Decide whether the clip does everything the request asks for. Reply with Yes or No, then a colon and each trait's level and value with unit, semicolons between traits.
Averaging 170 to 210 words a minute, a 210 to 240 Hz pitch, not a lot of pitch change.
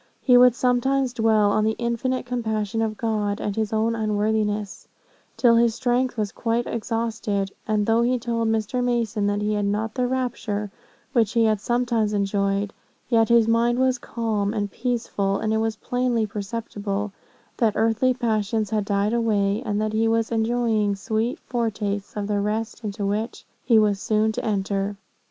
Yes: average, 175 wpm; high, 220 Hz; narrow, 2.2 semitones